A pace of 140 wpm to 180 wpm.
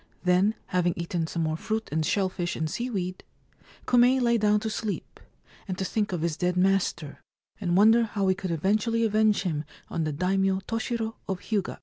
No: average, 190 wpm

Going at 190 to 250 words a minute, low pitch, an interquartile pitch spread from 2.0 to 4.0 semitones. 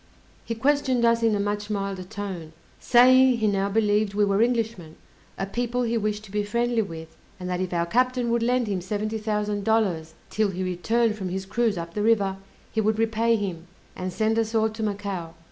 No: fast, 205 wpm; high, 210 Hz; average, 3.0 semitones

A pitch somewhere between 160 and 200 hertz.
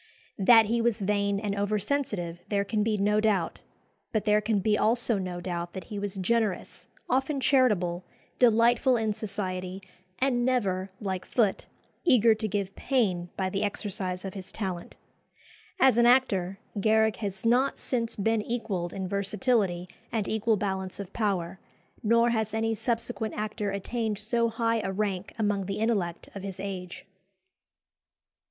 No: high, 210 Hz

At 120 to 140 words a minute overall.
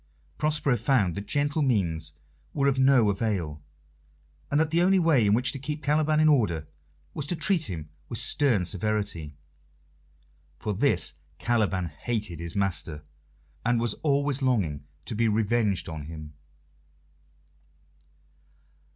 Yes: slow, 135 wpm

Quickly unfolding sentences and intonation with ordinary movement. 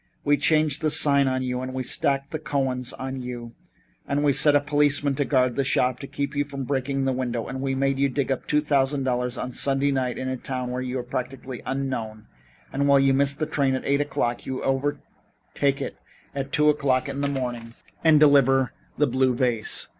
No: fast, 215 wpm; narrow, 1.7 semitones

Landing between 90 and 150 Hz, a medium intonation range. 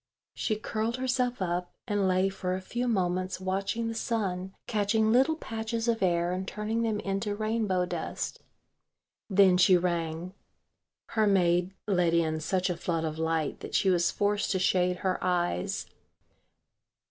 No: high, 190 Hz; average, 3.3 semitones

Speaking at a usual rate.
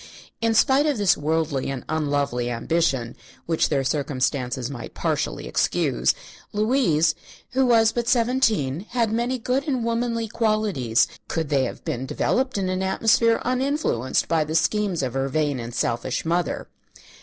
Yes: average, 150 wpm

